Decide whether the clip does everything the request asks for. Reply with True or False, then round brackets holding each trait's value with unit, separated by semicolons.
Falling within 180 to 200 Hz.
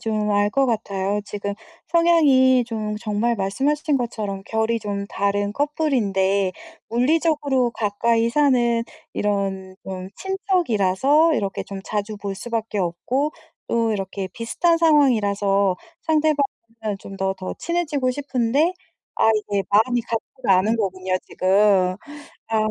False (220 Hz)